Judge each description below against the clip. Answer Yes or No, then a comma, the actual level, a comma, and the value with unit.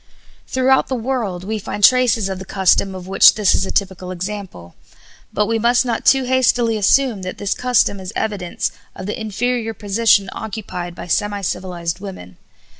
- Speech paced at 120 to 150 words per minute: No, average, 175 wpm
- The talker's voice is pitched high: Yes, high, 205 Hz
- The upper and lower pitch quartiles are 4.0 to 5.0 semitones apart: No, average, 3.6 semitones